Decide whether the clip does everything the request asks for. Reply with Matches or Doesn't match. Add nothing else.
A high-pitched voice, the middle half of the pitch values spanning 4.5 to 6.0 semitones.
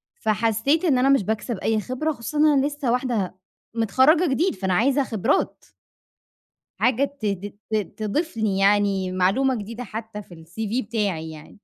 Matches